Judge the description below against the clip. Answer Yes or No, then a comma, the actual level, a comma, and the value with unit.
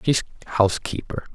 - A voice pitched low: Yes, low, 110 Hz